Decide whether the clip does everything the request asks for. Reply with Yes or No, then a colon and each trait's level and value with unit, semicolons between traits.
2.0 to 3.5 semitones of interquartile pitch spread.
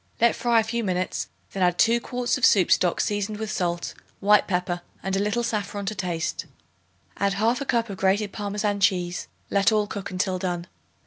Yes: average, 3.0 semitones